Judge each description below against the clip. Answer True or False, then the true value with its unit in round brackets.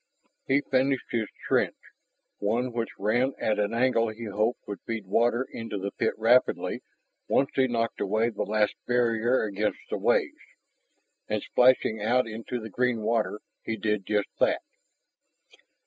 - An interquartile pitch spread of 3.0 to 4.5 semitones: False (2.6 semitones)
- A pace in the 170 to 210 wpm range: False (150 wpm)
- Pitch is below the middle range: True (115 Hz)